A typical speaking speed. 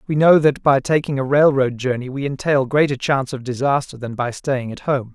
No: fast, 220 wpm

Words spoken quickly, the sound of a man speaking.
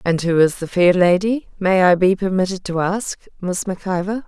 No: fast, 210 wpm; female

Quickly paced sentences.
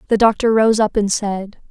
Yes: fast, 210 wpm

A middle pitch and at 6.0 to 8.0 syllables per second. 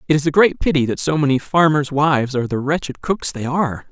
Yes: medium, 145 Hz; 6.2 syllables/s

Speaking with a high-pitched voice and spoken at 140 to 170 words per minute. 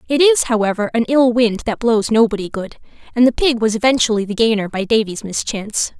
No: high, 225 Hz; average, 200 wpm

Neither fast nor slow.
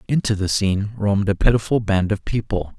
Yes: average, 195 wpm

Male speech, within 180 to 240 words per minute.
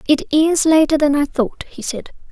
No: female; fast, 205 wpm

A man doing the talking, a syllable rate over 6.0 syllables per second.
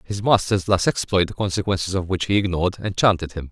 Yes: male; 6.2 syllables/s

